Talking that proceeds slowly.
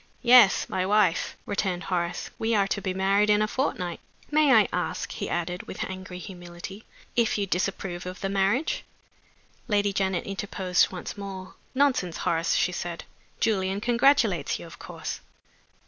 No: average, 155 wpm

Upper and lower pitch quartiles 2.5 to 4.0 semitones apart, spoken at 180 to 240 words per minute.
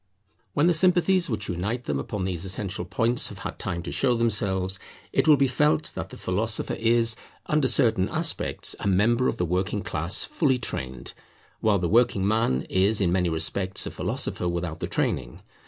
No: average, 5.1 semitones; average, 185 wpm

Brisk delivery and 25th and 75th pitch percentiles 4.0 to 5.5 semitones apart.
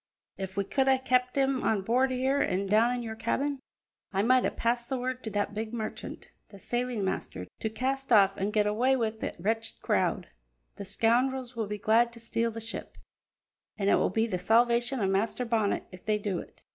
No: fast, 210 wpm; average, 3.3 semitones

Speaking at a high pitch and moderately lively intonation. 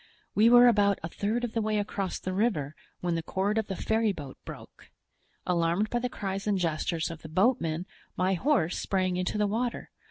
Yes: high, 195 Hz; average, 4.0 semitones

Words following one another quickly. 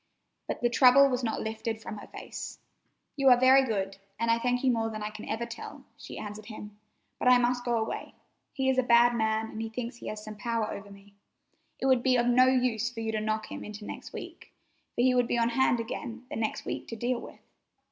Yes: fast, 240 wpm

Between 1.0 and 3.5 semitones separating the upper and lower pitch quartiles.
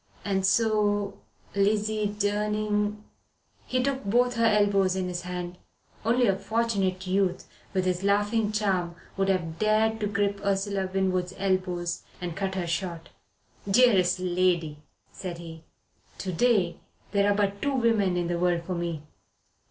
Yes: narrow, 2.6 semitones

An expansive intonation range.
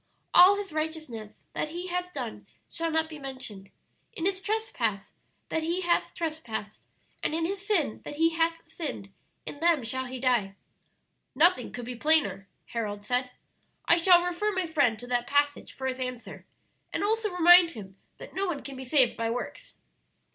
Yes: wide, 5.9 semitones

